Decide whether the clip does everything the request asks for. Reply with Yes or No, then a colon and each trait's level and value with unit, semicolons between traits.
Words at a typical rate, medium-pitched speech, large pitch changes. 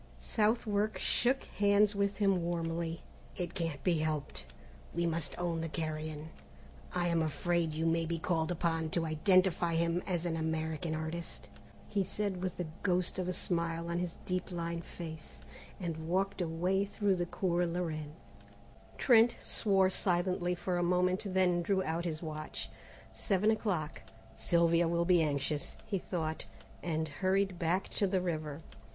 No: average, 160 wpm; medium, 170 Hz; narrow, 2.4 semitones